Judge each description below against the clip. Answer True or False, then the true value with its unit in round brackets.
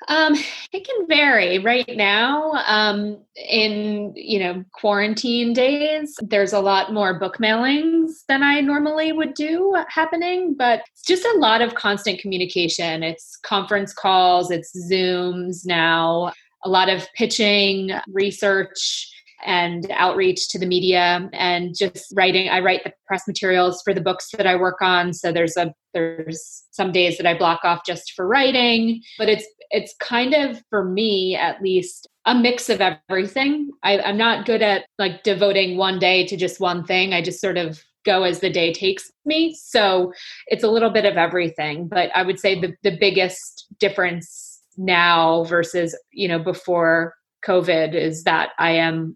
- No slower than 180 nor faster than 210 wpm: False (165 wpm)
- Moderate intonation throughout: True (4.3 semitones)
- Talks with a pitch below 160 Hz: False (195 Hz)